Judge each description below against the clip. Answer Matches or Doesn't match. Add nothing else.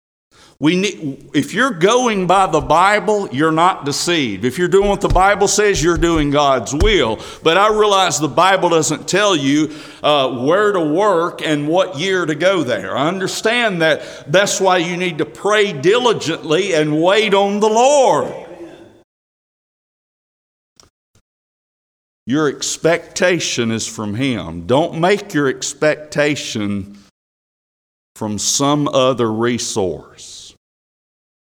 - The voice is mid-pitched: Matches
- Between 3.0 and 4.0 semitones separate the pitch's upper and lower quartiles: Doesn't match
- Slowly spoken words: Matches